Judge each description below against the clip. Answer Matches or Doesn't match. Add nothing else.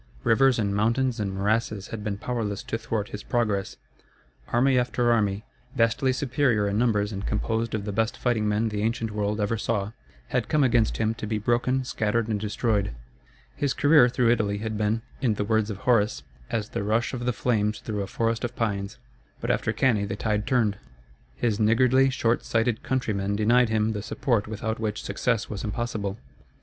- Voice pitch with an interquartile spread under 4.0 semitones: Matches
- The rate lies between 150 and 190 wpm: Matches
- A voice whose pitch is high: Doesn't match